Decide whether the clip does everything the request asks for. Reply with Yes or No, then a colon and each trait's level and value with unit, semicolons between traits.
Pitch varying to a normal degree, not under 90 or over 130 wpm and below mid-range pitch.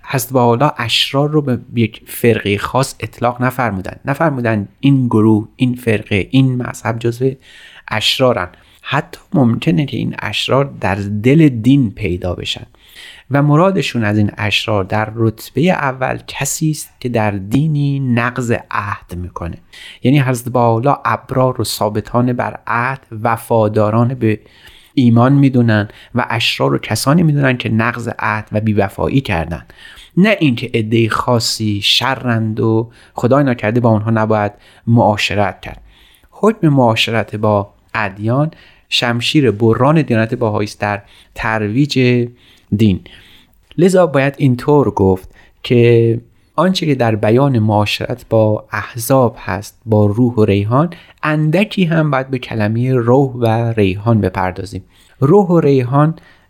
Yes: average, 4.0 semitones; average, 125 wpm; low, 115 Hz